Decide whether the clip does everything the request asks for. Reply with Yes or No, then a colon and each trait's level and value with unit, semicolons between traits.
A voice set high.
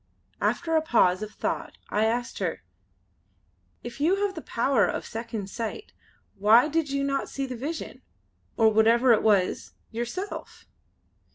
Yes: high, 240 Hz